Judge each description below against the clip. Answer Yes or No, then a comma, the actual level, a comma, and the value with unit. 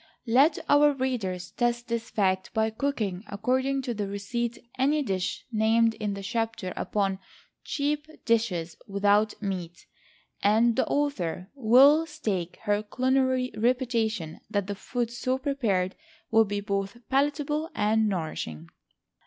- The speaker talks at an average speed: No, slow, 130 wpm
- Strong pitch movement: No, average, 4.7 semitones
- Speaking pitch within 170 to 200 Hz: No, high, 225 Hz